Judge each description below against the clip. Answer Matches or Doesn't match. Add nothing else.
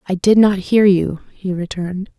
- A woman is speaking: Matches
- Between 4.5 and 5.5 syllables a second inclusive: Matches